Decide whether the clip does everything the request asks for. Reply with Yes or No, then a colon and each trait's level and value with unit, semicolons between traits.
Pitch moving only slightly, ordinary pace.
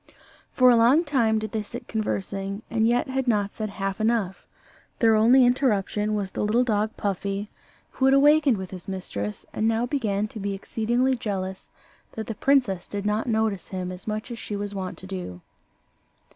No: average, 3.2 semitones; average, 185 wpm